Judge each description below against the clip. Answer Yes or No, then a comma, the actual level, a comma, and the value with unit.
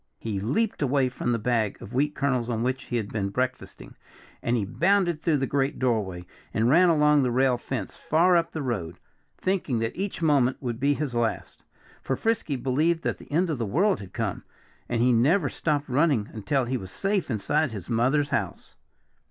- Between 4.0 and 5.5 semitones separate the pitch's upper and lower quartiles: Yes, average, 4.8 semitones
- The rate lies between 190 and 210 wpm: Yes, average, 200 wpm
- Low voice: Yes, low, 130 Hz